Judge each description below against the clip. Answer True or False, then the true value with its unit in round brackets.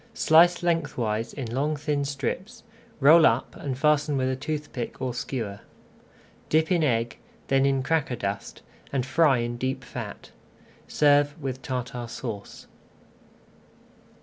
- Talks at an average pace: False (130 wpm)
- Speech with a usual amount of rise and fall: True (3.6 semitones)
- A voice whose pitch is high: False (135 Hz)